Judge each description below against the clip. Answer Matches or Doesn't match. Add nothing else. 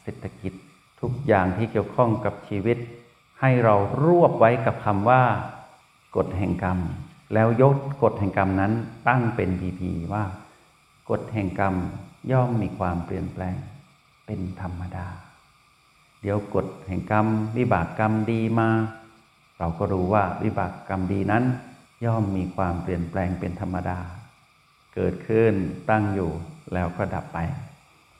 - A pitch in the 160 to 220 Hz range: Doesn't match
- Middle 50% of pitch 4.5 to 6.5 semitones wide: Doesn't match